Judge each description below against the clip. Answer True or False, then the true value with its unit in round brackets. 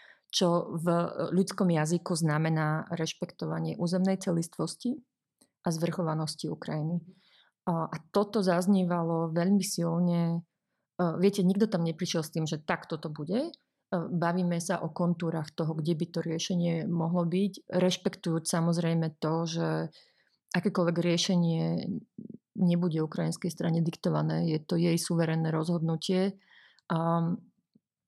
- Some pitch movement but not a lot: False (1.9 semitones)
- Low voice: False (170 Hz)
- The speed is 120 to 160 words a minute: False (110 wpm)